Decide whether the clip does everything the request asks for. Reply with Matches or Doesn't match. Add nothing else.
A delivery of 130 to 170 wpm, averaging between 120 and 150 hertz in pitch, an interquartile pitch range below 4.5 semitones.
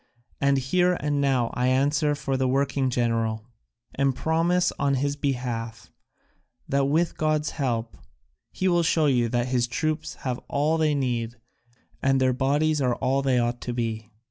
Matches